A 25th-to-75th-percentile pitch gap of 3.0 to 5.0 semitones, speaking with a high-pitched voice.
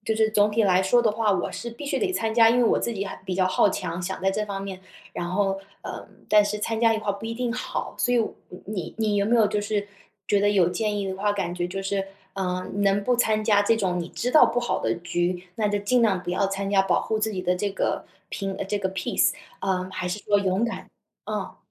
No: narrow, 2.6 semitones; high, 205 Hz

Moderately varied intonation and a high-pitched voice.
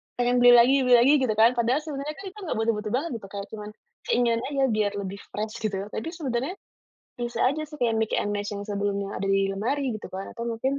Yes: average, 4.4 semitones; high, 235 Hz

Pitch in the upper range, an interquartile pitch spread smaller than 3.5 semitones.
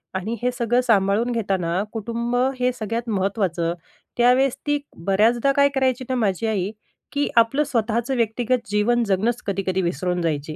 No: high, 225 Hz; average, 4.1 semitones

